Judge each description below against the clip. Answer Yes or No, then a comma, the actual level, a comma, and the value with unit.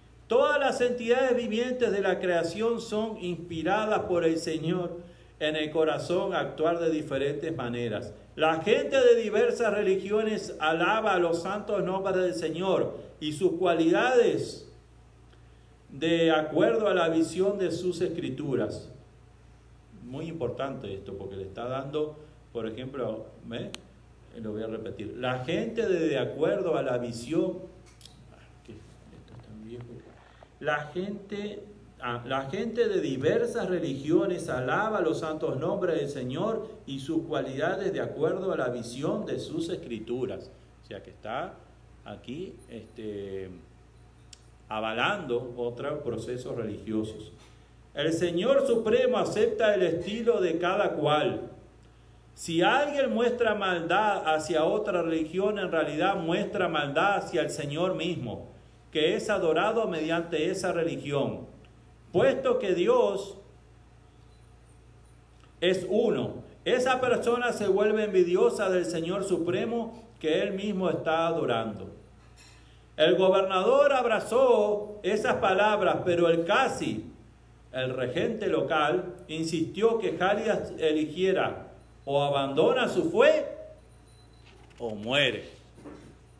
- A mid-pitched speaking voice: Yes, medium, 170 Hz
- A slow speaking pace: Yes, slow, 120 wpm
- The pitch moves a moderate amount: No, wide, 7.0 semitones